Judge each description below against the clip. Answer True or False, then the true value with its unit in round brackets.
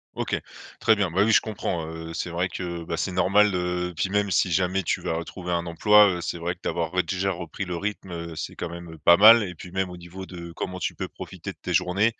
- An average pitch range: False (2.1 semitones)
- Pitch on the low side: True (90 Hz)